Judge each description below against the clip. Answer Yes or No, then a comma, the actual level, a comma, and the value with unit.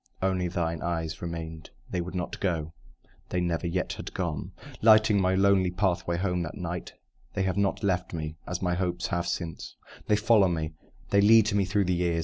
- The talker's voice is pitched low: Yes, very low, 90 Hz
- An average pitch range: No, narrow, 2.3 semitones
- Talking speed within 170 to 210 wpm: Yes, average, 190 wpm